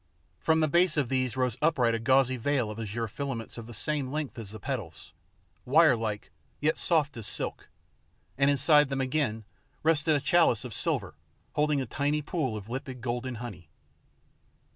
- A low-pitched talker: Yes, low, 130 Hz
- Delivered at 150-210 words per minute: Yes, average, 170 wpm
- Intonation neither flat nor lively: Yes, average, 4.4 semitones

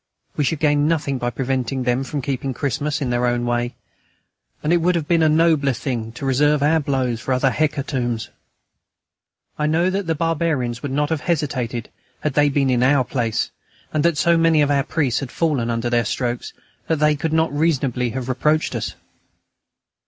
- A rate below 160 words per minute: No, average, 190 wpm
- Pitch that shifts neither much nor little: Yes, average, 3.9 semitones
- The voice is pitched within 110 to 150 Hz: Yes, medium, 140 Hz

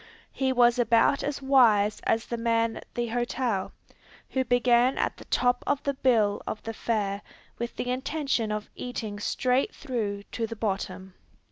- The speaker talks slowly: No, average, 160 wpm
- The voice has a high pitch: Yes, high, 235 Hz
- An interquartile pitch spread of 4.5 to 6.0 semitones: No, average, 3.0 semitones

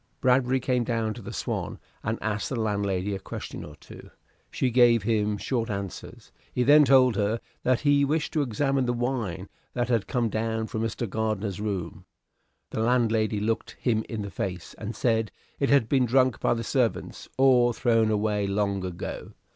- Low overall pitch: Yes, low, 115 Hz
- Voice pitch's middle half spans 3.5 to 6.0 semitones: No, average, 3.1 semitones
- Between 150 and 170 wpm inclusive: No, average, 180 wpm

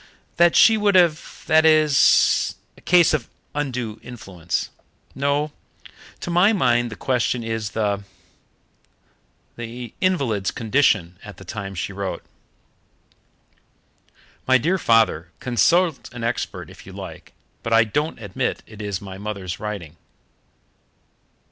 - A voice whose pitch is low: Yes, low, 120 Hz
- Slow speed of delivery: Yes, slow, 130 wpm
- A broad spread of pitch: Yes, wide, 6.7 semitones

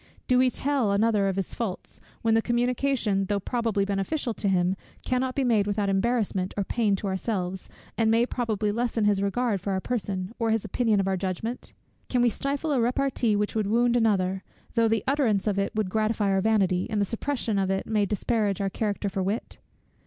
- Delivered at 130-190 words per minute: No, fast, 205 wpm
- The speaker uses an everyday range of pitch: Yes, average, 3.3 semitones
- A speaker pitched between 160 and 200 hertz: No, high, 215 Hz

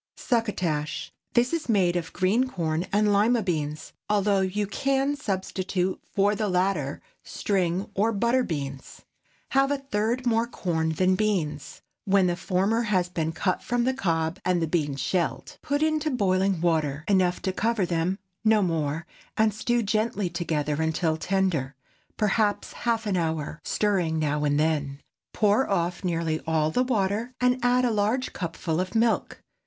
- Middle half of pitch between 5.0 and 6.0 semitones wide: Yes, average, 5.3 semitones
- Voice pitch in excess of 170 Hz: Yes, high, 190 Hz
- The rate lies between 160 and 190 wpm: No, average, 150 wpm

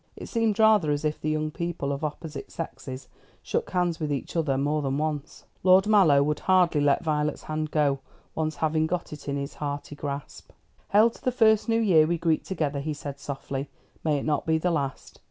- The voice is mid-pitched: Yes, medium, 155 Hz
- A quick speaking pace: Yes, fast, 210 wpm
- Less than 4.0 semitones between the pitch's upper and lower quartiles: Yes, average, 3.4 semitones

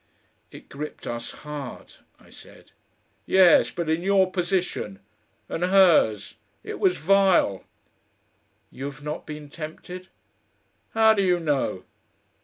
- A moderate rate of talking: No, slow, 115 wpm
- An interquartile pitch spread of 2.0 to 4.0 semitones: No, average, 4.5 semitones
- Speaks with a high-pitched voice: No, medium, 170 Hz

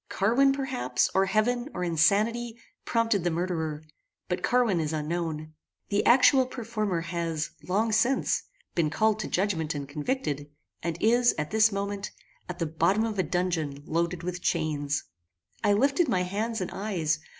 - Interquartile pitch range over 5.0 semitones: Yes, wide, 5.5 semitones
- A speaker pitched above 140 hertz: Yes, medium, 185 Hz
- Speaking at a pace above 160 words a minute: No, average, 155 wpm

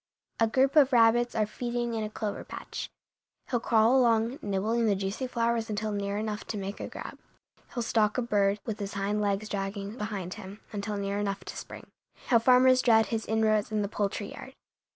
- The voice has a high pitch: Yes, high, 215 Hz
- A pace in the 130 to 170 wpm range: No, average, 195 wpm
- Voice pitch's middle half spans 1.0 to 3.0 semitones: Yes, narrow, 2.6 semitones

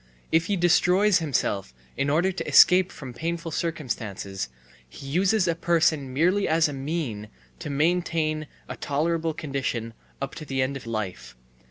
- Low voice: No, medium, 155 Hz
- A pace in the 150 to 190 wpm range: Yes, average, 155 wpm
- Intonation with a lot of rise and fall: No, average, 4.5 semitones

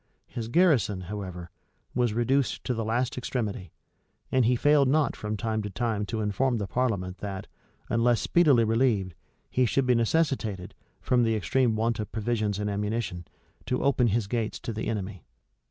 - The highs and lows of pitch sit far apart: No, average, 3.3 semitones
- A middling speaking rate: Yes, average, 170 wpm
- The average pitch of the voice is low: Yes, low, 115 Hz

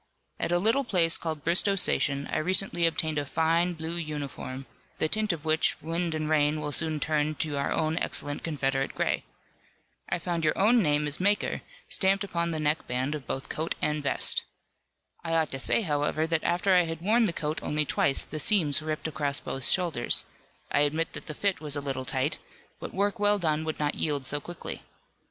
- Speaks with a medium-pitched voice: Yes, medium, 155 Hz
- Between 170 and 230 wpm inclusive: Yes, average, 200 wpm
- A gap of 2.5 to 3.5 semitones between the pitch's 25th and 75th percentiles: Yes, average, 2.9 semitones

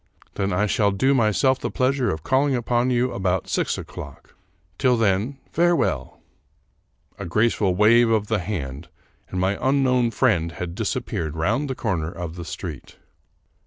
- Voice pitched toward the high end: No, low, 105 Hz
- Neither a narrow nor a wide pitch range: No, wide, 6.0 semitones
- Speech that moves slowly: No, average, 160 wpm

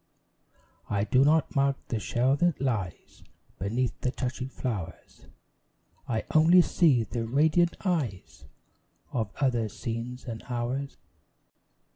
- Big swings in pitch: No, average, 3.6 semitones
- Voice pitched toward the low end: Yes, low, 125 Hz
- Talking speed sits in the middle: No, slow, 115 wpm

